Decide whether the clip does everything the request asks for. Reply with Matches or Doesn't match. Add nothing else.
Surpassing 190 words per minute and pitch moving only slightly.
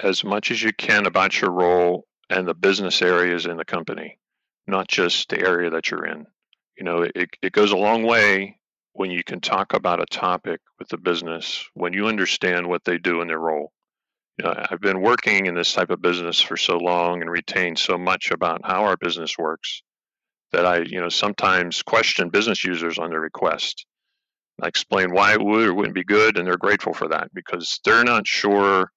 Matches